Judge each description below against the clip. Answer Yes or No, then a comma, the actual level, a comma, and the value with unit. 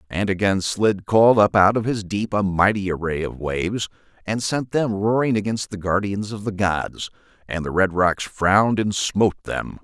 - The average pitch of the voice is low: Yes, low, 100 Hz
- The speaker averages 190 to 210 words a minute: Yes, average, 195 wpm